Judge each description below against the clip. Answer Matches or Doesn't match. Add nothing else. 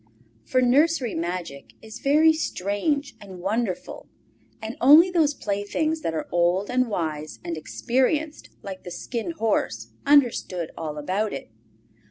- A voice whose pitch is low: Doesn't match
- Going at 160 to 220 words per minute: Doesn't match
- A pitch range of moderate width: Doesn't match